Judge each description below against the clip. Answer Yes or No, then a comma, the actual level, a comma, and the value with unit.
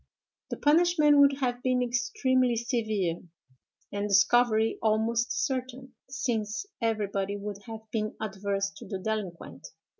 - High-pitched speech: Yes, high, 225 Hz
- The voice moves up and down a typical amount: Yes, average, 3.7 semitones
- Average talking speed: No, slow, 120 wpm